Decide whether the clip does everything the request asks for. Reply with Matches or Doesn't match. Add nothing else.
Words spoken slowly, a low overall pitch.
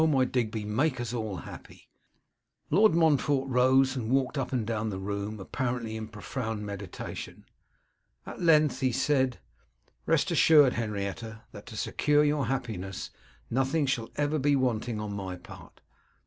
Doesn't match